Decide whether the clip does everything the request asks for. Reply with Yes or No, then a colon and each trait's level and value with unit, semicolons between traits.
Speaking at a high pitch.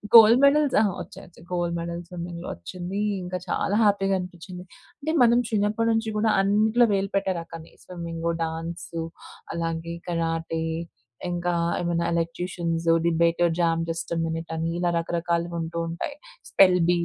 No: medium, 175 Hz